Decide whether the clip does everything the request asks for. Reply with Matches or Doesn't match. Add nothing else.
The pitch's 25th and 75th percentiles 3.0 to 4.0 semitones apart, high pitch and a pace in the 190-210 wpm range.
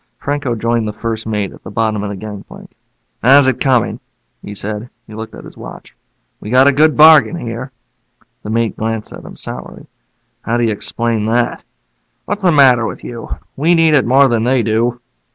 Doesn't match